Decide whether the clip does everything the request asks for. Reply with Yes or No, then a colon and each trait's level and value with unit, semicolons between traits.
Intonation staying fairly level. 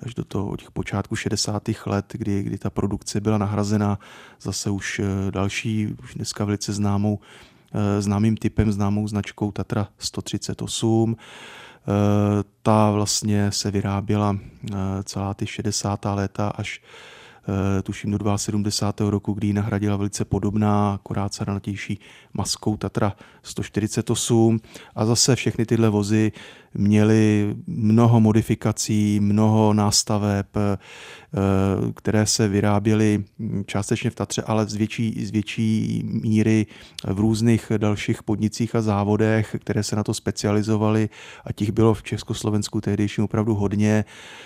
Yes: narrow, 1.3 semitones